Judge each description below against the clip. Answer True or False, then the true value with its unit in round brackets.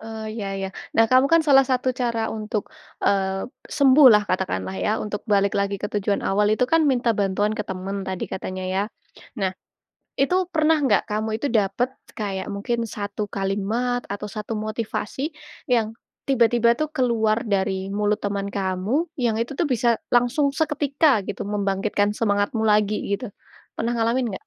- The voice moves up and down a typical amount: True (3.6 semitones)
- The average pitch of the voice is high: True (215 Hz)